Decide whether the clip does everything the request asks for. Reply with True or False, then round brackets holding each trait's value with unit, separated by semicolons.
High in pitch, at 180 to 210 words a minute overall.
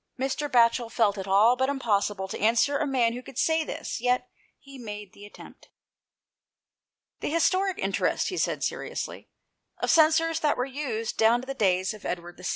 True (245 Hz; 190 wpm)